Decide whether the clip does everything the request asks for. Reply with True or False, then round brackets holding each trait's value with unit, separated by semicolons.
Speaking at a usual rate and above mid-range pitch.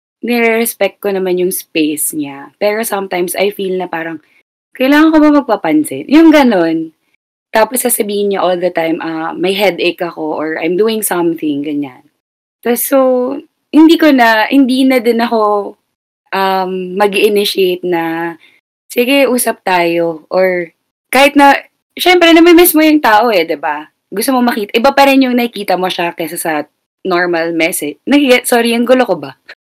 False (165 wpm; 200 Hz)